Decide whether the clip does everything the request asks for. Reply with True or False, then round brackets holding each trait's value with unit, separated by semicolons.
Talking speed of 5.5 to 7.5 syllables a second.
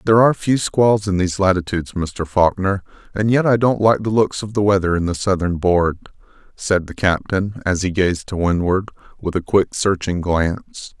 False (5.1 syllables/s)